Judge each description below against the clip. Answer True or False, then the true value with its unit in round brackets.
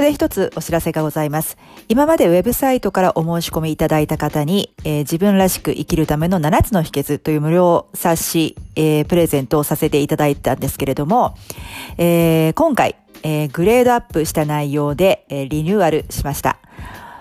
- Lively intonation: False (3.0 semitones)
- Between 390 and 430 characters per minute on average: False (340 characters per minute)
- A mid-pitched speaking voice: True (160 Hz)